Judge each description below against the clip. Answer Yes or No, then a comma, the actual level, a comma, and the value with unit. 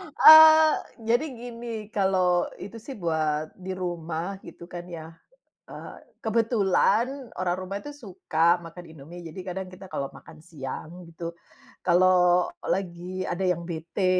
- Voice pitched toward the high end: No, medium, 180 Hz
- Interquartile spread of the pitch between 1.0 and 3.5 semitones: Yes, average, 2.8 semitones